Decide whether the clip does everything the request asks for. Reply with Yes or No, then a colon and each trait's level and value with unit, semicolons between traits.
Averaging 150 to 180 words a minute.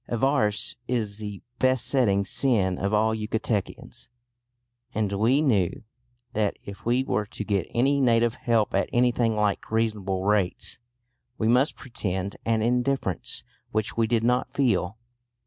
No: slow, 135 wpm